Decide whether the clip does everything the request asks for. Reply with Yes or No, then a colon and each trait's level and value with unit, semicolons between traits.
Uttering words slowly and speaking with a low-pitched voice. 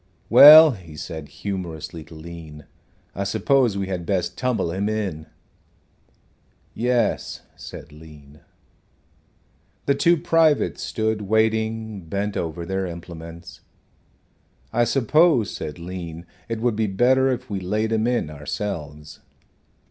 Yes: slow, 120 wpm; low, 100 Hz